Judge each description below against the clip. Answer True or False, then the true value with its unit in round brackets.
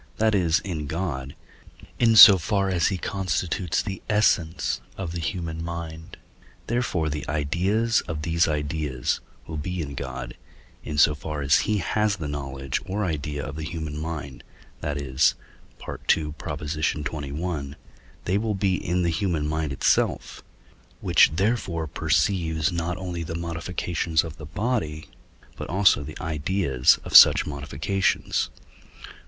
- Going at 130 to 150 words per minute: True (140 wpm)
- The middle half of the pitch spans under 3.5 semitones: False (3.8 semitones)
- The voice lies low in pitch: True (80 Hz)